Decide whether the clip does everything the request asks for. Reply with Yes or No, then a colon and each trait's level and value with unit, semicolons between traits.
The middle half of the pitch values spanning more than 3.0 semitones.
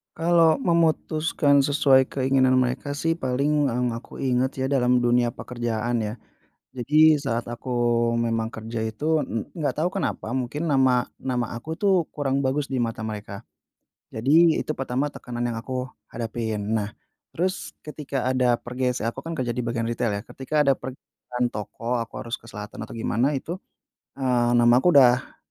Yes: average, 3.4 semitones